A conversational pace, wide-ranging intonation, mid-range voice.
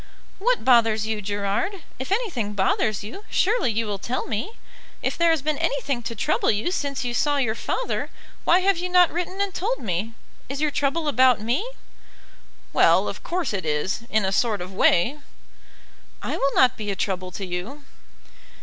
No: average, 185 wpm; wide, 8.5 semitones; very high, 250 Hz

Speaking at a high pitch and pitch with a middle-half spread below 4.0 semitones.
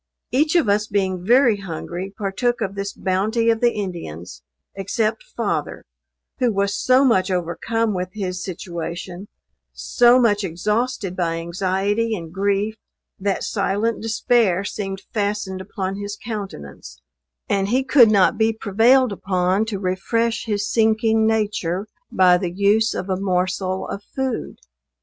Yes: high, 200 Hz; average, 3.1 semitones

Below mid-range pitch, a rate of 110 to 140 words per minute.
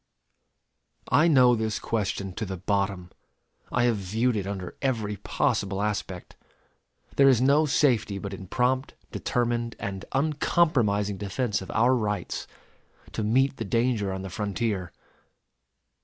Yes: low, 110 Hz; slow, 135 wpm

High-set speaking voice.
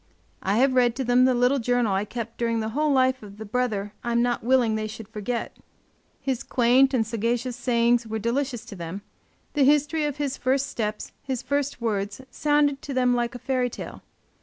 Yes: high, 245 Hz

